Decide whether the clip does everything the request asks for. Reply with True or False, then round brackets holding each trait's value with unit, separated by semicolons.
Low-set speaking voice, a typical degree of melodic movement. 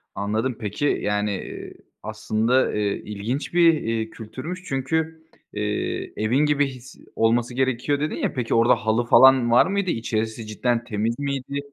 True (120 Hz; 3.7 semitones)